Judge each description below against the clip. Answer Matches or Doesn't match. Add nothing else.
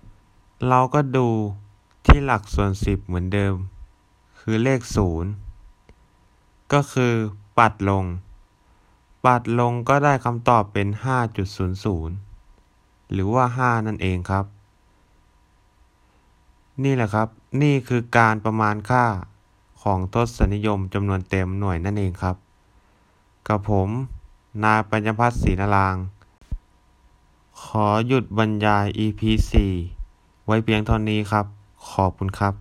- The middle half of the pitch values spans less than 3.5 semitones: Matches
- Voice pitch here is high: Doesn't match